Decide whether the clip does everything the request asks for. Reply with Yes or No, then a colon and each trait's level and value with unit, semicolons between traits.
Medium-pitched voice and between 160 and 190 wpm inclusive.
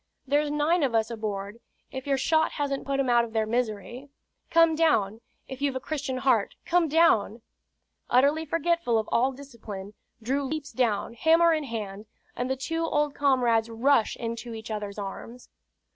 No: very high, 255 Hz; average, 170 wpm